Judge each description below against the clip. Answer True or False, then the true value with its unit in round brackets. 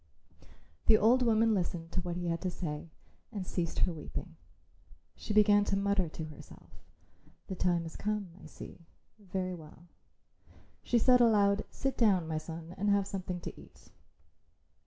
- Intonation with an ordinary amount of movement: True (3.6 semitones)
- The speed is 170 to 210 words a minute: False (160 wpm)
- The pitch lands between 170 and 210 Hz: True (185 Hz)